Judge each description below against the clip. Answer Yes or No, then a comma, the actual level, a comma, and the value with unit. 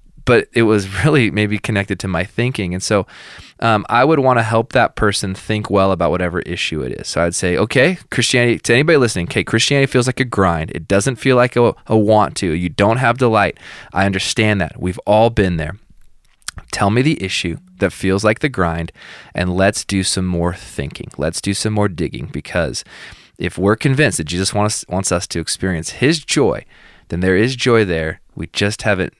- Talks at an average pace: No, fast, 210 wpm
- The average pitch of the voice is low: Yes, low, 100 Hz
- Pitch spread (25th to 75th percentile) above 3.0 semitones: Yes, average, 4.4 semitones